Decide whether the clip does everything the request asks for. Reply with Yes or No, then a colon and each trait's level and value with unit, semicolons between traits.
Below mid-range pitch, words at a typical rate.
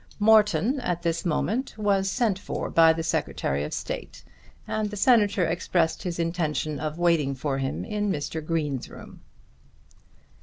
No: medium, 170 Hz; average, 150 wpm